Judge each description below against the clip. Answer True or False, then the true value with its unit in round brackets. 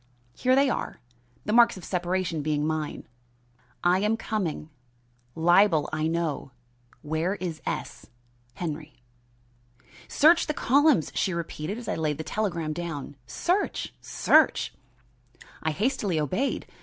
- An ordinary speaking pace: False (125 wpm)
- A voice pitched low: False (175 Hz)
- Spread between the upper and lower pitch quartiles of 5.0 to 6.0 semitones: True (5.4 semitones)